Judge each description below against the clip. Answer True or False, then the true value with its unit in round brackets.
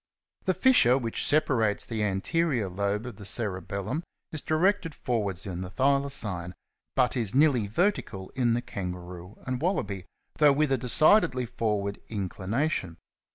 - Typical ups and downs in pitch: False (6.1 semitones)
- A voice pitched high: False (115 Hz)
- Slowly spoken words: False (145 wpm)